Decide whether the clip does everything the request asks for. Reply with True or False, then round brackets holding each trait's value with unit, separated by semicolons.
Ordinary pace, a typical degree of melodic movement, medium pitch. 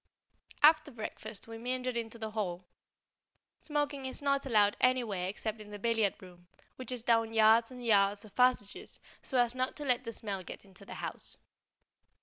False (175 wpm; 3.6 semitones; 225 Hz)